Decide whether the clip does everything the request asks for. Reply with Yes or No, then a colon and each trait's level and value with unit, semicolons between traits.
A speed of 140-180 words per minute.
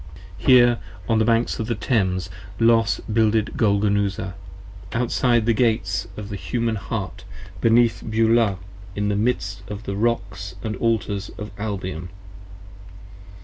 Yes: average, 145 wpm